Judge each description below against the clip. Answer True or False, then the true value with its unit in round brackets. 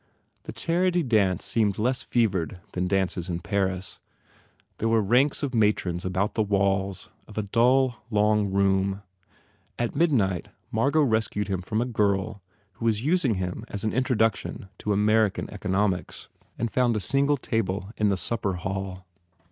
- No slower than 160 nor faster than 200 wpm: True (165 wpm)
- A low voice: True (105 Hz)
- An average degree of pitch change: True (3.4 semitones)